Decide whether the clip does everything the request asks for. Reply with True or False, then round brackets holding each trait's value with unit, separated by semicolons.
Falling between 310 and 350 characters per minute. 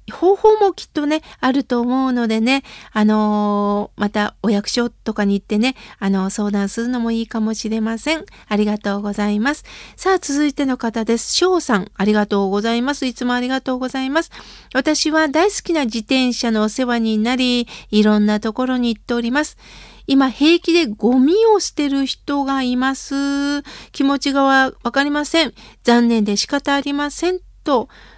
True (335 characters per minute)